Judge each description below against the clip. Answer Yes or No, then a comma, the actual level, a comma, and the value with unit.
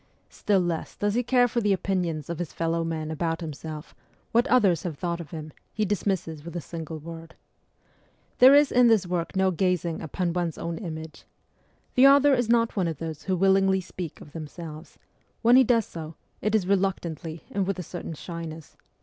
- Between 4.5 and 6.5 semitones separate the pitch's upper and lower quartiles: No, average, 3.7 semitones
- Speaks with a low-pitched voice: No, medium, 175 Hz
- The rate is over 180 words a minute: Yes, average, 190 wpm